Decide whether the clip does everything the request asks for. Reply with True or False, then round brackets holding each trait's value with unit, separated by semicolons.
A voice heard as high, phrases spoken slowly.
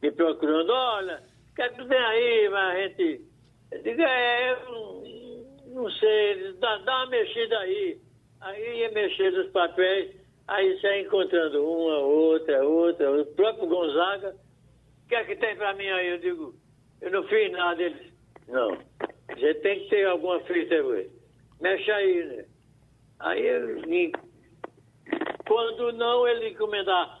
False (235 Hz; 155 wpm)